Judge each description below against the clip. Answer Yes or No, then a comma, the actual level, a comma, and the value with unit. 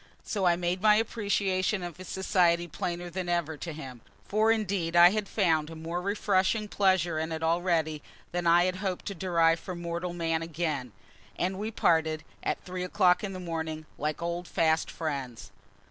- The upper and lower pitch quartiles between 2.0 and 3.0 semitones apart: Yes, narrow, 2.4 semitones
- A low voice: No, medium, 175 Hz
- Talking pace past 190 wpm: No, average, 180 wpm